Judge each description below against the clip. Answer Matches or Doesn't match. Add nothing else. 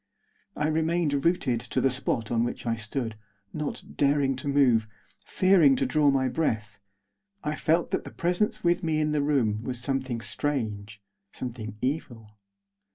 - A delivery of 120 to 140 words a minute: Doesn't match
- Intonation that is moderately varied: Matches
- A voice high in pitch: Doesn't match